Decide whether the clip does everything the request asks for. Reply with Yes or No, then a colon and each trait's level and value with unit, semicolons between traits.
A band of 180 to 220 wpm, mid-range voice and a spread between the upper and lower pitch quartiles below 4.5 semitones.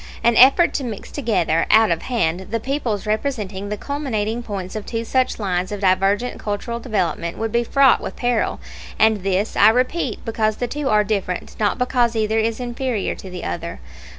No: average, 185 wpm; high, 220 Hz; average, 3.4 semitones